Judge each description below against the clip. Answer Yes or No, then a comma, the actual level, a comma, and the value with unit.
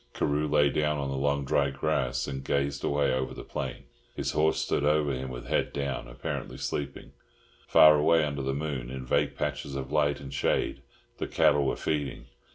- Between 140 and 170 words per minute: No, average, 190 wpm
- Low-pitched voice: Yes, very low, 70 Hz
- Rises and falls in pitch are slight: Yes, narrow, 1.6 semitones